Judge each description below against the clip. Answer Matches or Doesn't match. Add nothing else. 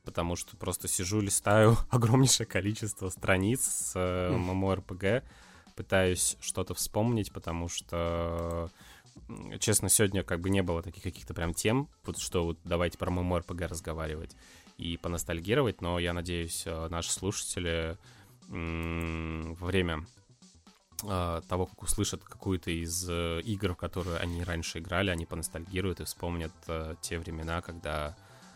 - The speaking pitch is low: Matches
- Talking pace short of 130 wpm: Doesn't match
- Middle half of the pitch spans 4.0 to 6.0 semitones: Doesn't match